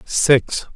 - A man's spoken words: Yes, male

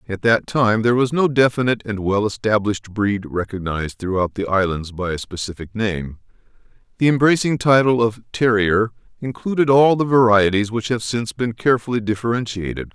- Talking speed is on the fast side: No, average, 160 wpm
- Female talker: No, male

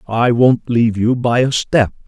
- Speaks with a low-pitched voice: Yes, low, 120 Hz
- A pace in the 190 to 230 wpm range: Yes, average, 200 wpm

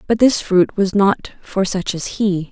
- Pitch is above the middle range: Yes, high, 195 Hz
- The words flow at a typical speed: No, fast, 215 wpm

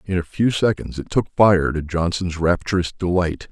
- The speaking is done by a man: Yes, male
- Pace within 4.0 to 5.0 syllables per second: Yes, 4.9 syllables/s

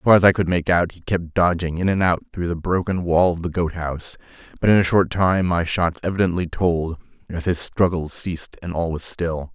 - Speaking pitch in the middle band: No, very low, 85 Hz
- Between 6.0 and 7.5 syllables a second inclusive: No, 5.4 syllables/s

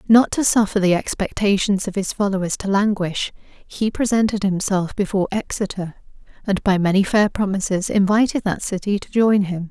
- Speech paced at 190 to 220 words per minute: No, average, 160 wpm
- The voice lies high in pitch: Yes, high, 200 Hz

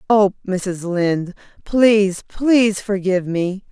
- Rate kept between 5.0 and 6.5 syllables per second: No, 4.0 syllables/s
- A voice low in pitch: No, high, 195 Hz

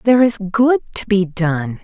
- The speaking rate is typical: Yes, average, 195 wpm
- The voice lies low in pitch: No, high, 205 Hz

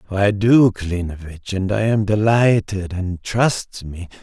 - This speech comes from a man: Yes, male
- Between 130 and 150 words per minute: Yes, average, 140 wpm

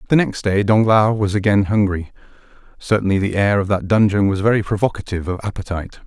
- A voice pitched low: Yes, low, 100 Hz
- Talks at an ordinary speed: Yes, average, 180 wpm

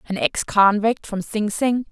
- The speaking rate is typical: Yes, average, 190 wpm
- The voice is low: No, high, 210 Hz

